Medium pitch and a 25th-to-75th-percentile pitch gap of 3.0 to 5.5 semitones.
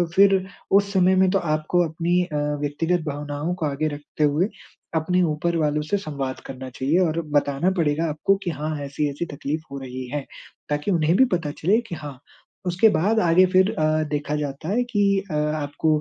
Yes: medium, 155 Hz; average, 3.5 semitones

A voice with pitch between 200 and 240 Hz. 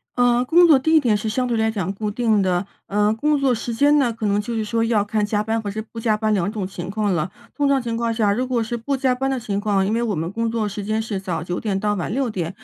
Yes: high, 220 Hz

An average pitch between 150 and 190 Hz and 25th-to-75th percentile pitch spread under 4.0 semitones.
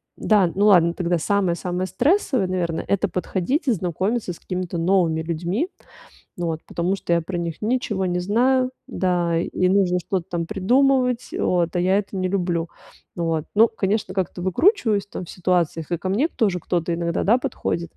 Yes: medium, 185 Hz; average, 3.3 semitones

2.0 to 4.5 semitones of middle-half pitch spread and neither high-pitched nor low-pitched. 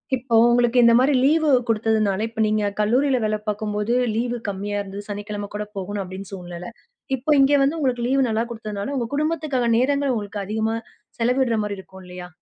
No: average, 3.6 semitones; high, 220 Hz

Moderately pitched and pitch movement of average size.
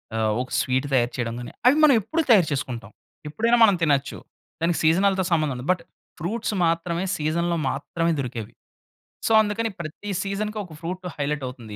No: medium, 165 Hz; wide, 6.5 semitones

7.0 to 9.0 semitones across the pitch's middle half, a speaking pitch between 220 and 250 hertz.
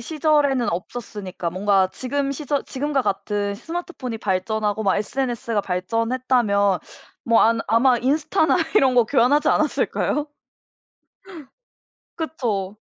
No: wide, 5.4 semitones; high, 235 Hz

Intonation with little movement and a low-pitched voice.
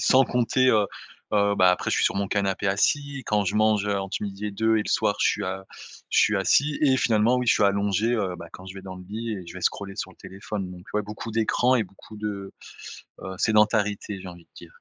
Yes: narrow, 2.3 semitones; low, 105 Hz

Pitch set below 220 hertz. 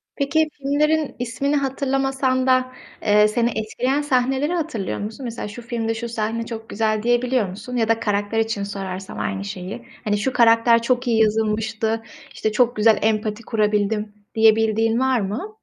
No: high, 225 Hz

